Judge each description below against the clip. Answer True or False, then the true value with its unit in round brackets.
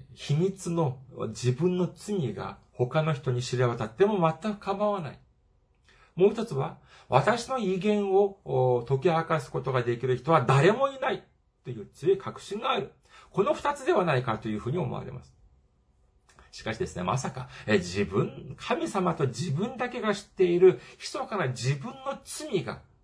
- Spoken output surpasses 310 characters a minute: False (295 characters per minute)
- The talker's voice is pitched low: False (165 Hz)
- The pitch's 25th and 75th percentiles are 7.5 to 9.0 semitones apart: True (8.4 semitones)